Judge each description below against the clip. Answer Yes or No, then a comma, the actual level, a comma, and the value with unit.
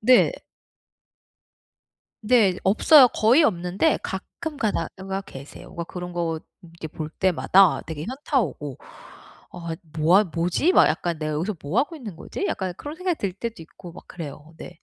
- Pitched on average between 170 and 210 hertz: Yes, medium, 185 Hz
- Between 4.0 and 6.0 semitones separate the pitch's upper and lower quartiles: Yes, wide, 5.5 semitones